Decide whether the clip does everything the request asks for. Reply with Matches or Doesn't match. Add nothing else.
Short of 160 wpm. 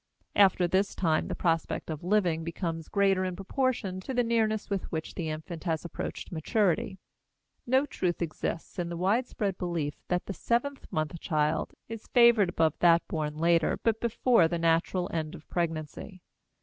Doesn't match